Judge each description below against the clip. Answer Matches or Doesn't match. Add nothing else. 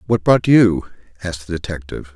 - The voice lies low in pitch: Matches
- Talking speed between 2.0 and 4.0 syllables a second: Doesn't match